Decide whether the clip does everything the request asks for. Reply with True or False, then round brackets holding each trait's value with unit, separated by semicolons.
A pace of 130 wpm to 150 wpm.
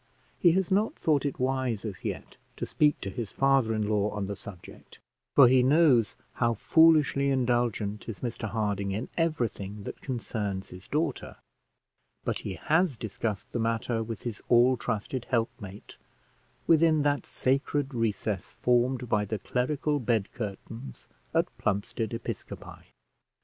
True (145 wpm)